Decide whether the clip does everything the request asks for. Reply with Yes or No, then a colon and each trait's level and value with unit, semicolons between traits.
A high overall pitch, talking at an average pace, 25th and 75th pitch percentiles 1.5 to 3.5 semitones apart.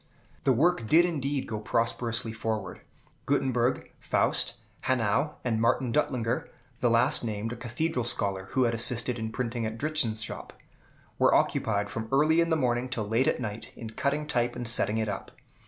No: low, 120 Hz; average, 170 wpm; average, 3.0 semitones